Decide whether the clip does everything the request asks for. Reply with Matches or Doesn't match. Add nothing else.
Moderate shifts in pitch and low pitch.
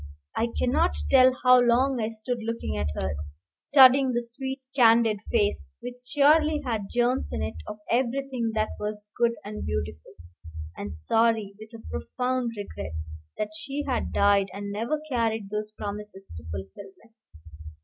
Doesn't match